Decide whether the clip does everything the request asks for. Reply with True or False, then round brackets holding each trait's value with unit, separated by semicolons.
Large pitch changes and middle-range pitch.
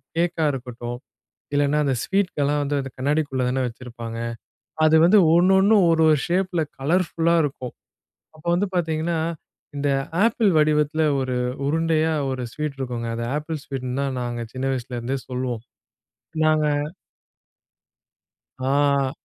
False (3.9 semitones; 145 Hz)